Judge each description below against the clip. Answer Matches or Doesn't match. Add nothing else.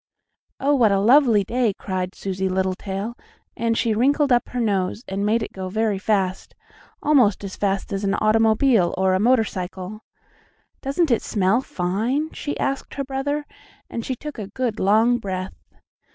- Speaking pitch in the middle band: Doesn't match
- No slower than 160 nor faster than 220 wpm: Matches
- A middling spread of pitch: Matches